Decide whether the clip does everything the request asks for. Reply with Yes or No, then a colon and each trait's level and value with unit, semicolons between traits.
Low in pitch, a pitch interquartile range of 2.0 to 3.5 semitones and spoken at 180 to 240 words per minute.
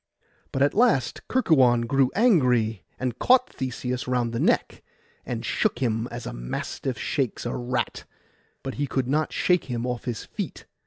No: low, 125 Hz; average, 2.8 semitones; average, 165 wpm